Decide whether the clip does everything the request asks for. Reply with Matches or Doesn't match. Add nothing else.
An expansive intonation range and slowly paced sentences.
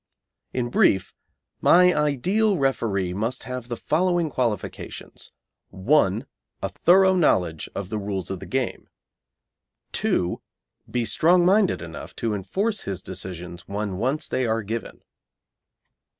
Matches